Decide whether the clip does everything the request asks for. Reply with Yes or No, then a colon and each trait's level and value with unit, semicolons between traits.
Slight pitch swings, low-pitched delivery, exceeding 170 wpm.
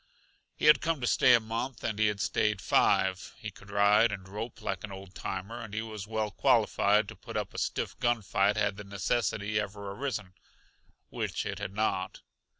Yes: narrow, 2.2 semitones; low, 105 Hz; average, 200 wpm